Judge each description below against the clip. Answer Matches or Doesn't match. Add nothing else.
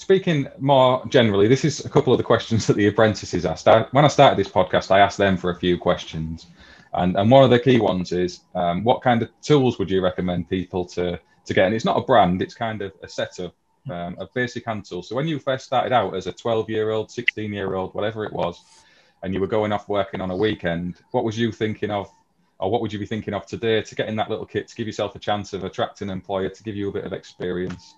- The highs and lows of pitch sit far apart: Doesn't match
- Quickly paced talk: Matches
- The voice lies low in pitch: Matches